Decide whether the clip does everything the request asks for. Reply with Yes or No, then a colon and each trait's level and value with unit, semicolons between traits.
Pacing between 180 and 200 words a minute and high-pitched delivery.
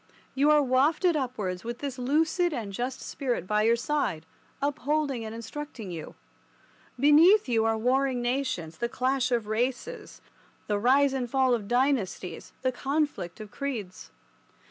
No: average, 145 wpm; very high, 255 Hz